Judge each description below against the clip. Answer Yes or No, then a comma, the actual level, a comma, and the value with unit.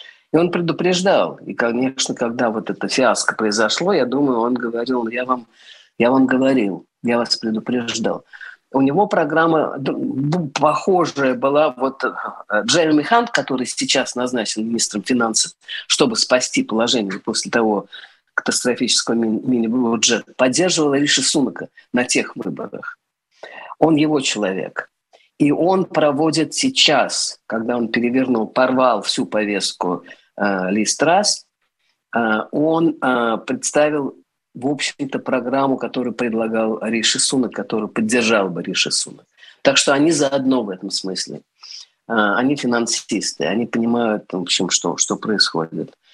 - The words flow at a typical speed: Yes, average, 125 wpm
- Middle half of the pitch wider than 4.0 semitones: Yes, average, 4.7 semitones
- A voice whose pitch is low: Yes, low, 130 Hz